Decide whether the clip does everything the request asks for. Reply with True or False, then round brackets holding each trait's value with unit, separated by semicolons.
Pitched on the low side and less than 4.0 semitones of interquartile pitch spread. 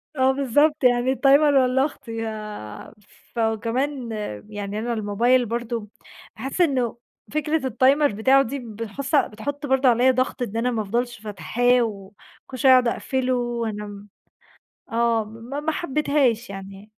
False (240 Hz; 3.4 semitones)